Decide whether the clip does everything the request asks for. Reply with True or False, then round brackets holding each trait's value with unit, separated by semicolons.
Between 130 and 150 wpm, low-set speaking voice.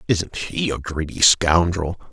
True (140 wpm; 85 Hz)